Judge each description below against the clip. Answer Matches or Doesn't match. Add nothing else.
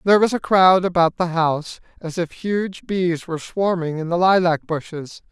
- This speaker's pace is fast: Doesn't match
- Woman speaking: Doesn't match